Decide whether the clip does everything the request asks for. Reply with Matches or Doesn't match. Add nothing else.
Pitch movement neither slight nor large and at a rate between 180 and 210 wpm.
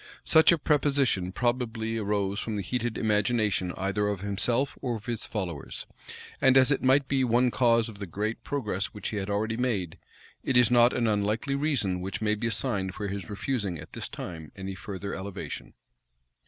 Matches